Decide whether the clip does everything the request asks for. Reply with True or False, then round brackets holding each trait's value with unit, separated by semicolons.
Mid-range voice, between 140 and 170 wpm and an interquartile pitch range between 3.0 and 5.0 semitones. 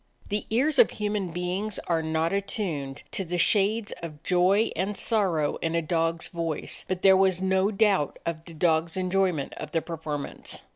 False (180 Hz; 180 wpm; 3.4 semitones)